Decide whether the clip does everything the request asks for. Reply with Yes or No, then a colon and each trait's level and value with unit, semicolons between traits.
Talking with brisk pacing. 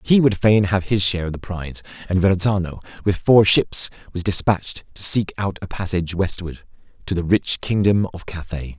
No: average, 190 wpm